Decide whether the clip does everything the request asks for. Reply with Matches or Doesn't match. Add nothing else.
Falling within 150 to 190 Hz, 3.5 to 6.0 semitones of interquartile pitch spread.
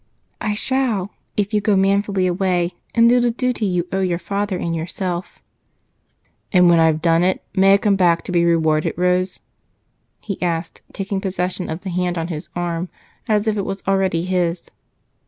Doesn't match